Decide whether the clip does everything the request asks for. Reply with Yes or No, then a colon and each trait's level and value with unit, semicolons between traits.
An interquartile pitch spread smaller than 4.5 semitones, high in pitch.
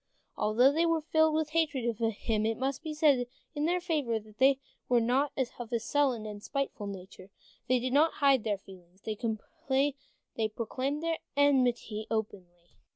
No: average, 5.1 semitones; very high, 250 Hz